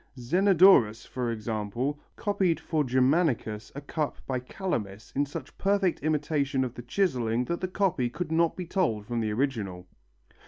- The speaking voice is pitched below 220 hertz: Yes, low, 135 Hz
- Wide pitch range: Yes, wide, 6.7 semitones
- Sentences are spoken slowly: No, average, 155 wpm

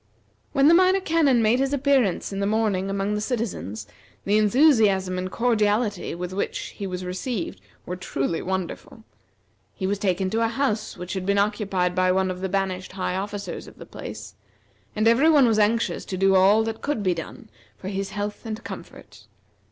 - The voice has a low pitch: No, high, 205 Hz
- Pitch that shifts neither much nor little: Yes, average, 3.4 semitones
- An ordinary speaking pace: Yes, average, 190 wpm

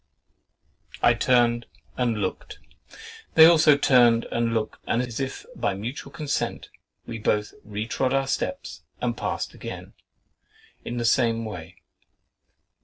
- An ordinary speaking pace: No, slow, 120 wpm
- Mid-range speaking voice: No, low, 120 Hz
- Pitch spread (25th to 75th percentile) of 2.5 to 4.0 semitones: Yes, average, 3.2 semitones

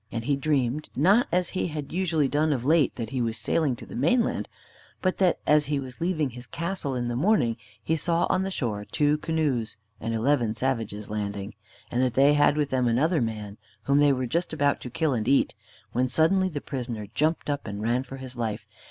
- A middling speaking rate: No, fast, 215 wpm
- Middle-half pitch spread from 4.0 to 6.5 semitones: Yes, average, 4.7 semitones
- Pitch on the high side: No, low, 135 Hz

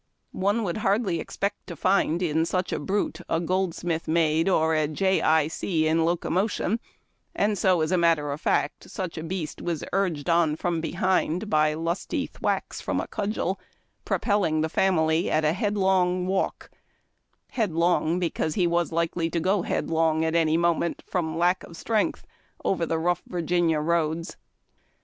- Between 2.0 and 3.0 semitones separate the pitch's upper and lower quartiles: Yes, average, 2.7 semitones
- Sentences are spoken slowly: No, average, 165 wpm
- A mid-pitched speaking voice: Yes, medium, 170 Hz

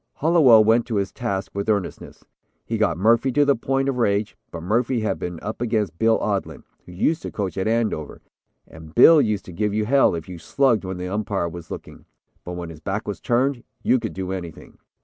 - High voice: No, low, 105 Hz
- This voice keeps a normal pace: No, fast, 215 wpm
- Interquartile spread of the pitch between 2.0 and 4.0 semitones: No, average, 4.6 semitones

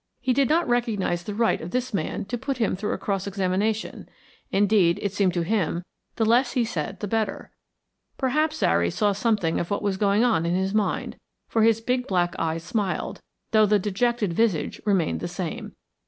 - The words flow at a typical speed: Yes, average, 195 wpm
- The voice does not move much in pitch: No, average, 3.9 semitones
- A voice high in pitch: Yes, high, 205 Hz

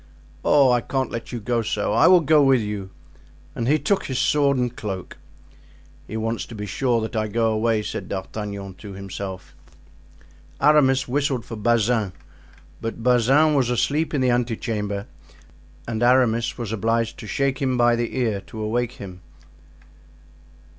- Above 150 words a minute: Yes, average, 165 wpm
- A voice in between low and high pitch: No, low, 115 Hz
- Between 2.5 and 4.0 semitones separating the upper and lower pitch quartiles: Yes, average, 3.4 semitones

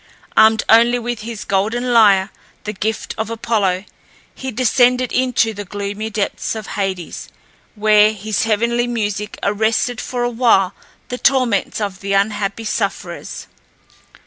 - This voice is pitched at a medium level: No, high, 220 Hz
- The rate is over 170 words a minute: No, slow, 135 wpm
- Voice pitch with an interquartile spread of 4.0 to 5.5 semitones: No, average, 2.7 semitones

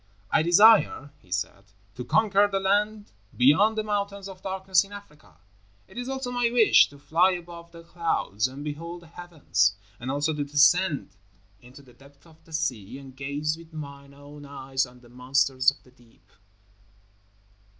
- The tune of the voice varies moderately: No, wide, 6.0 semitones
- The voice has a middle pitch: Yes, medium, 155 Hz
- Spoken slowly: No, average, 170 wpm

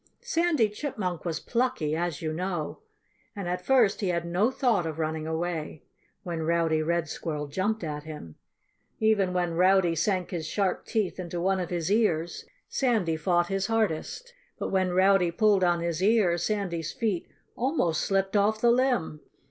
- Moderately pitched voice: Yes, medium, 180 Hz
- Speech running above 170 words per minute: No, average, 165 wpm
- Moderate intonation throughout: Yes, average, 4.2 semitones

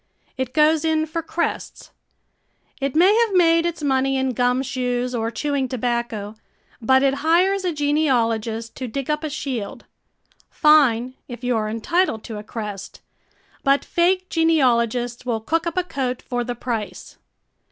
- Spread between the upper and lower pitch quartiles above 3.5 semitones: Yes, average, 4.9 semitones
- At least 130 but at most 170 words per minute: Yes, average, 155 wpm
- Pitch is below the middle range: No, very high, 265 Hz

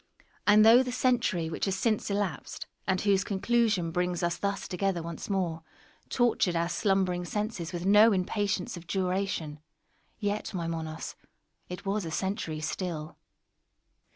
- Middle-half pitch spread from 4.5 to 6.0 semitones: No, average, 3.3 semitones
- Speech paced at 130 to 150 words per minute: Yes, average, 145 wpm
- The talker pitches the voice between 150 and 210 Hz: Yes, high, 190 Hz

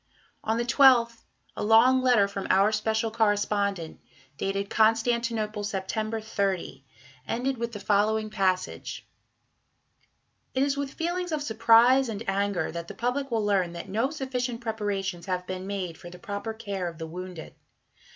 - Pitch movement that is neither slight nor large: Yes, average, 3.2 semitones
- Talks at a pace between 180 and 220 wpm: No, average, 150 wpm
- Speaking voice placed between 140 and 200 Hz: No, high, 215 Hz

